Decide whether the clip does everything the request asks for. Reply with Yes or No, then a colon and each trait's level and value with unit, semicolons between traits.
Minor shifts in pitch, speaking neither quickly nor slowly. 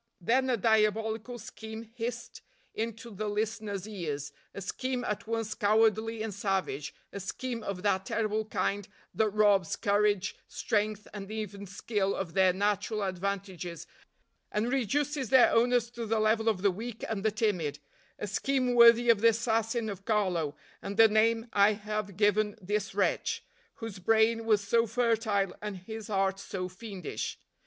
Yes: narrow, 2.3 semitones; average, 155 wpm